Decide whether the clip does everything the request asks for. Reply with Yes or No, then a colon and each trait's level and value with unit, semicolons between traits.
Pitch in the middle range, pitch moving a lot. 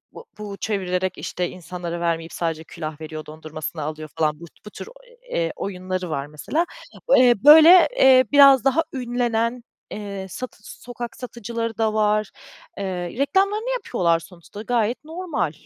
No: high, 205 Hz; wide, 6.8 semitones